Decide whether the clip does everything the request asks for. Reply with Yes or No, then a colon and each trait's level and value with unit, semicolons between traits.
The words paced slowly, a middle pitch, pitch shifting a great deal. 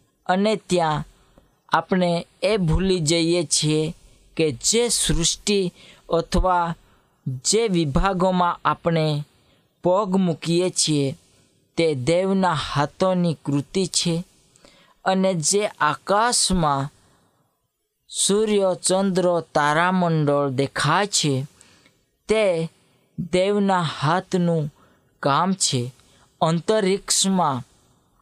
No: slow, 75 wpm; medium, 170 Hz; average, 3.9 semitones